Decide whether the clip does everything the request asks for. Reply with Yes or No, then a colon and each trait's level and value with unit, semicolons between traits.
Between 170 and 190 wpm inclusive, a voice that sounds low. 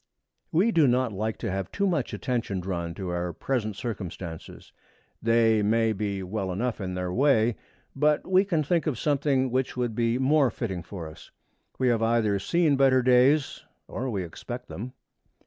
Yes: average, 175 wpm; low, 115 Hz